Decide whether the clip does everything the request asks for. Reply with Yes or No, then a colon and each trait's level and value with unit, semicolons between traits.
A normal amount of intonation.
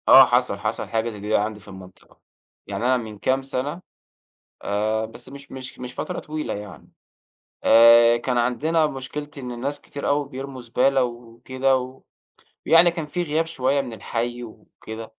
Yes: average, 3.4 semitones